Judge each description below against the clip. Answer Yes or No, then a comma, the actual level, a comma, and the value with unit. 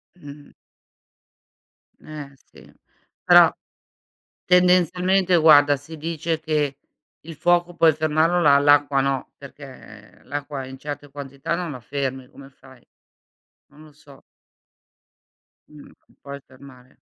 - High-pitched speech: No, medium, 145 Hz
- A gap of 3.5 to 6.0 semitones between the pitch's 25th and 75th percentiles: No, average, 2.7 semitones